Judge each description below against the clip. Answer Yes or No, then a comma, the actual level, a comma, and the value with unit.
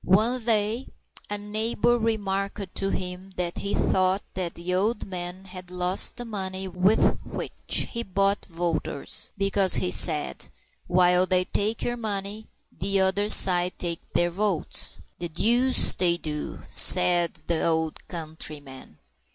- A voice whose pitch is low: No, high, 190 Hz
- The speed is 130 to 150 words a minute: Yes, average, 140 wpm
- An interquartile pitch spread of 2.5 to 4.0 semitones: Yes, average, 2.8 semitones